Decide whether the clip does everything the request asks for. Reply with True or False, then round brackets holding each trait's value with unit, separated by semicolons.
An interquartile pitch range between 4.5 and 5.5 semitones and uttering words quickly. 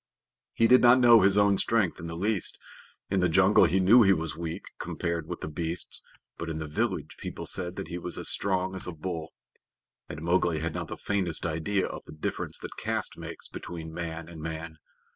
False (3.2 semitones; 210 wpm)